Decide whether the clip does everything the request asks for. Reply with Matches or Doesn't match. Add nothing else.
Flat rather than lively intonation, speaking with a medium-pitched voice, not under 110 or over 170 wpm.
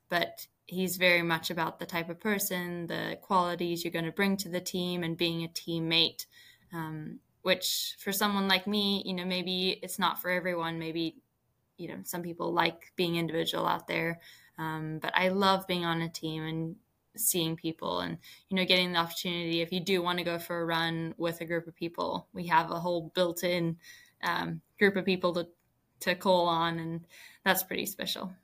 Doesn't match